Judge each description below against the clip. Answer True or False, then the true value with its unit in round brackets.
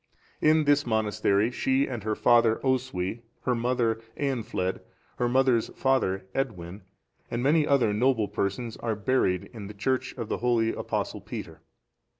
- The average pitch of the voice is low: True (120 Hz)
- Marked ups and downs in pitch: False (3.8 semitones)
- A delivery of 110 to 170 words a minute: True (150 wpm)